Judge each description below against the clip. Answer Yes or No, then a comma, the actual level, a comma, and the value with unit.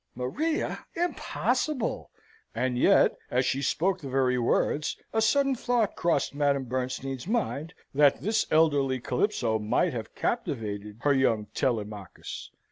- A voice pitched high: No, low, 135 Hz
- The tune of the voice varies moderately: No, wide, 6.8 semitones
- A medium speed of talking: No, slow, 125 wpm